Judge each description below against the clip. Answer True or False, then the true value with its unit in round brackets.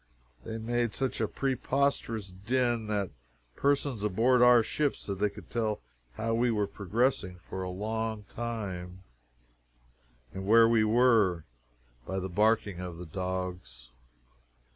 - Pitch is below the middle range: True (110 Hz)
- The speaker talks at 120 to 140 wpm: True (135 wpm)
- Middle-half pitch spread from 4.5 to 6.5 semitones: False (4.1 semitones)